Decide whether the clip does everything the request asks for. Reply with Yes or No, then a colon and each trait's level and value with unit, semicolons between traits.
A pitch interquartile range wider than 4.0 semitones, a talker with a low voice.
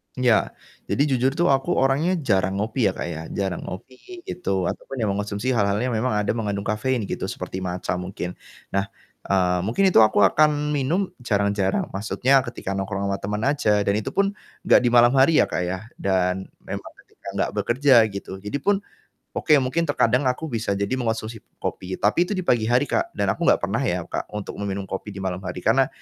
Yes: wide, 5.4 semitones; low, 110 Hz